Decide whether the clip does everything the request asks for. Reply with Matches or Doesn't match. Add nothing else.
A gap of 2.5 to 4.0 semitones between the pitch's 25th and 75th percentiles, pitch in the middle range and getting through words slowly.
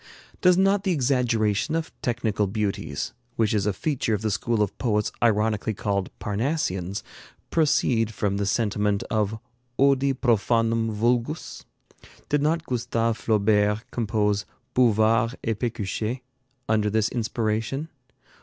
Doesn't match